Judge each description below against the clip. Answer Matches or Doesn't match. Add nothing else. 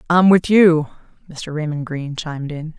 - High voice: Doesn't match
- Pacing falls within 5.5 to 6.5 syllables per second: Doesn't match